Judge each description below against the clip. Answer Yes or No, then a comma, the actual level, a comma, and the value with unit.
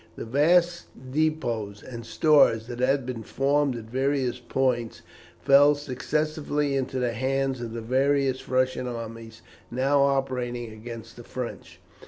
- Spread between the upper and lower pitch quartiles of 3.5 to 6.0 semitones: No, average, 2.9 semitones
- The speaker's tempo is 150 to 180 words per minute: No, slow, 135 wpm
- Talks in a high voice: No, low, 130 Hz